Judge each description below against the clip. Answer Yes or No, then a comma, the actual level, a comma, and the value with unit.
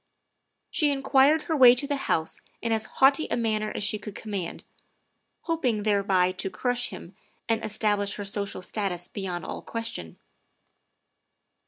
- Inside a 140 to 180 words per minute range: Yes, average, 150 wpm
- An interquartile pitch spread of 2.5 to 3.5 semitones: No, average, 4.1 semitones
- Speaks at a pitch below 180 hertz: No, high, 215 Hz